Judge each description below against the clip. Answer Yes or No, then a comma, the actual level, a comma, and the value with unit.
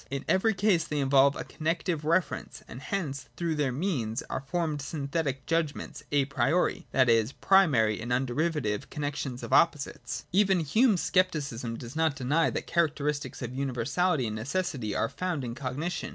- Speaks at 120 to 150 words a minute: No, average, 170 wpm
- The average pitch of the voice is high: No, medium, 145 Hz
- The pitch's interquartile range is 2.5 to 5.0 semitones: Yes, average, 4.7 semitones